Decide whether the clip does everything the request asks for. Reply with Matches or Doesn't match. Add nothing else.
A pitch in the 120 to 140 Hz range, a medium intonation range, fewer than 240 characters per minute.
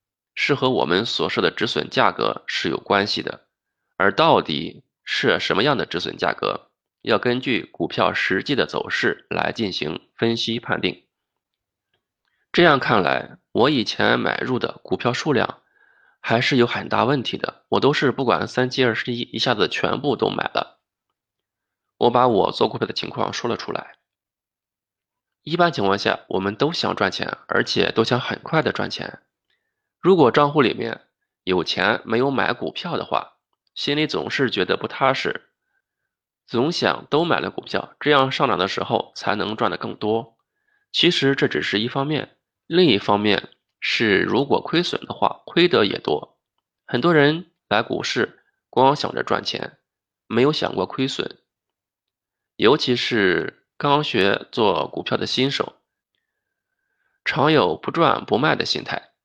Doesn't match